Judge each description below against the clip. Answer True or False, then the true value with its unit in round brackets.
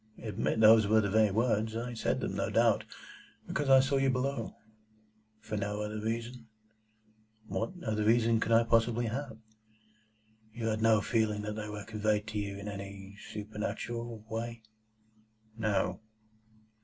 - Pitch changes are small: True (1.7 semitones)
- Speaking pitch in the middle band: False (110 Hz)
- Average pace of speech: True (150 wpm)